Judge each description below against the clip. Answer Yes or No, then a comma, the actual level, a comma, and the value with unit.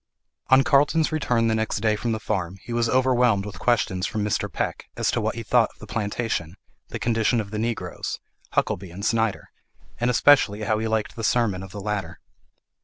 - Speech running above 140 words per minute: Yes, average, 200 wpm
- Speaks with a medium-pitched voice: No, low, 110 Hz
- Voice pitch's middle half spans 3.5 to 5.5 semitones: No, average, 2.9 semitones